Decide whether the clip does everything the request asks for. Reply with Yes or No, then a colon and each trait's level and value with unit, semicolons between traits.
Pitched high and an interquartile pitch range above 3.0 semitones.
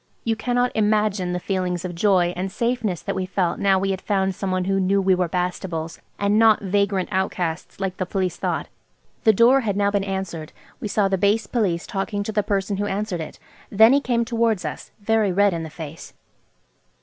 No: high, 195 Hz; narrow, 2.6 semitones